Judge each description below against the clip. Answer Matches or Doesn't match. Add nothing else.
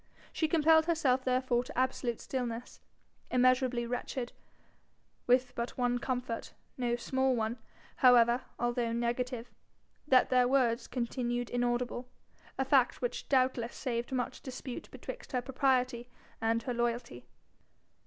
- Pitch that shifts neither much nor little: Doesn't match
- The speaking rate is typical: Doesn't match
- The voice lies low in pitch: Doesn't match